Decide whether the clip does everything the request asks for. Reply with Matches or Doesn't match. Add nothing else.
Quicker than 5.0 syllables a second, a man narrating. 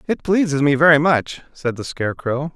Matches